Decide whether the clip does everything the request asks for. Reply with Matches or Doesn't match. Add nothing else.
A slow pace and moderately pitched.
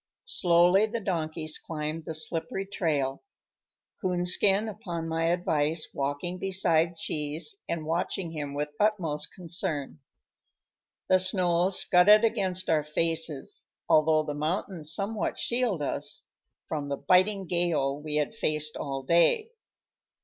Matches